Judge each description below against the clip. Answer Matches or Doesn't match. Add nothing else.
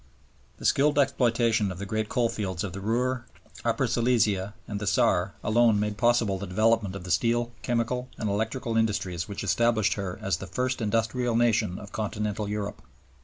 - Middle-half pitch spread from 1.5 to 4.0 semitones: Matches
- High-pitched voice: Doesn't match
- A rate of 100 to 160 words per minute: Doesn't match